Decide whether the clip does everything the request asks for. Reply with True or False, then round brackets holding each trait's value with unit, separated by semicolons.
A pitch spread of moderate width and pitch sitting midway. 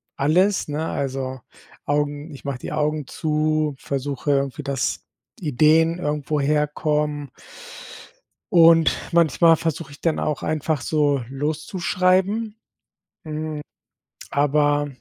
False (1.9 semitones; 150 Hz)